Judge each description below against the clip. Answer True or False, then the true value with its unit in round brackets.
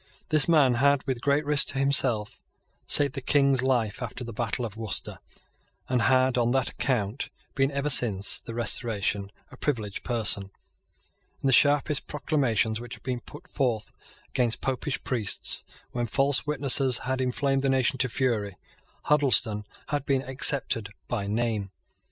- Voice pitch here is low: True (130 Hz)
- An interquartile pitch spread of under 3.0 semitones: False (3.4 semitones)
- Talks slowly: False (155 wpm)